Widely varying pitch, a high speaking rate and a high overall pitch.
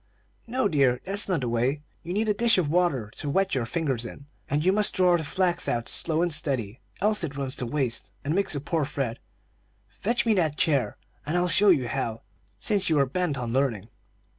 No: wide, 6.0 semitones; fast, 215 wpm; medium, 150 Hz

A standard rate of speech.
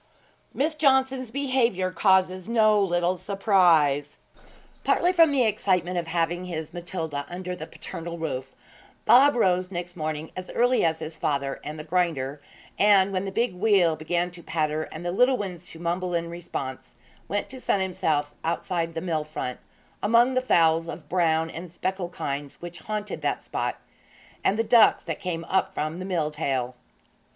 Yes: average, 170 wpm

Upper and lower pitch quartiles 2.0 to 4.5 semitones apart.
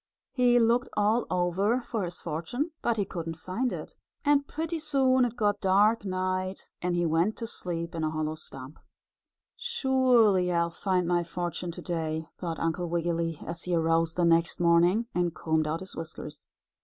No: average, 5.3 semitones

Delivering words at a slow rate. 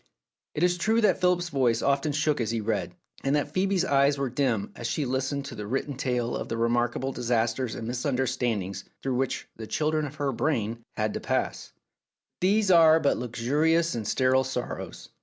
No: average, 195 wpm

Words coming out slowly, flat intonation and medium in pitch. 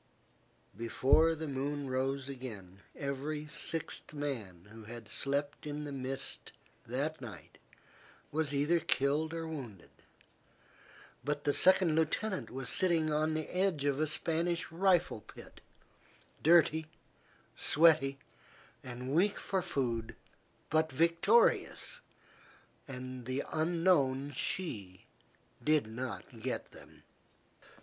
No: slow, 110 wpm; average, 3.7 semitones; medium, 145 Hz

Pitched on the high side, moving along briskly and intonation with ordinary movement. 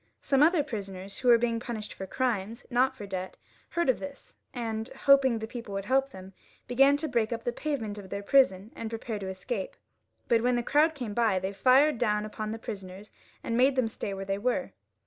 Yes: high, 230 Hz; fast, 215 wpm; average, 4.5 semitones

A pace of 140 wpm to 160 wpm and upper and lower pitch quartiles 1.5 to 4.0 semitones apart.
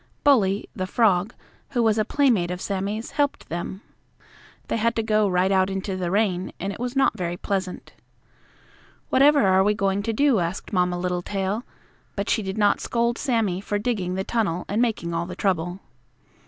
No: average, 180 wpm; average, 3.5 semitones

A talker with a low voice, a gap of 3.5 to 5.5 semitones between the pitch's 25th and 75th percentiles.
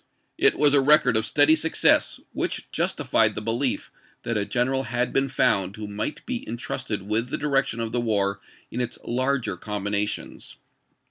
Yes: low, 120 Hz; average, 4.2 semitones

